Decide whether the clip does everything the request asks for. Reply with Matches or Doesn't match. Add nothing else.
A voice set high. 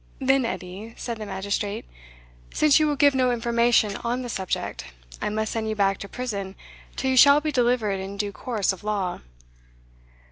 Matches